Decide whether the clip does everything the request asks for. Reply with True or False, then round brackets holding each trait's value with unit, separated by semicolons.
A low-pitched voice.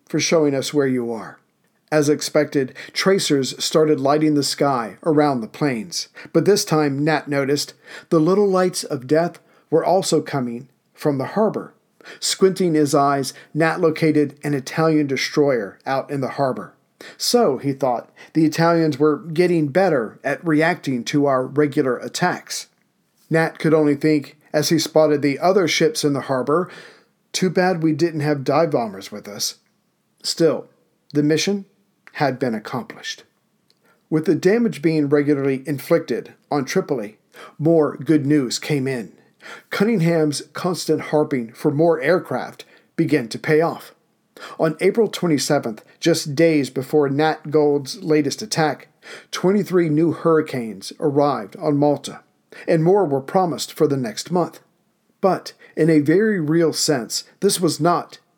False (155 Hz)